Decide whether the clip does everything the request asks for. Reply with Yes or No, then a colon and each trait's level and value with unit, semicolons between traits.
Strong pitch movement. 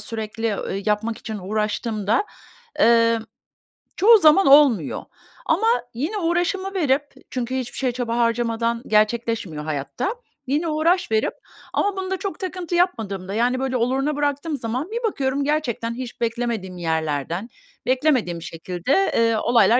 Yes: wide, 5.8 semitones